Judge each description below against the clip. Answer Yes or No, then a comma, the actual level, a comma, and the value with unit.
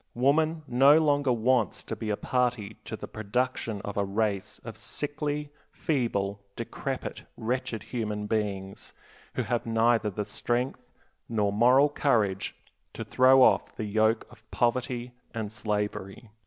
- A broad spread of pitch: No, average, 3.6 semitones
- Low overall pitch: Yes, low, 115 Hz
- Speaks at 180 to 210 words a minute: No, average, 140 wpm